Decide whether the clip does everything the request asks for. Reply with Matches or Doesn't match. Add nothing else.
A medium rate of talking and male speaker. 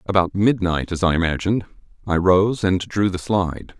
Matches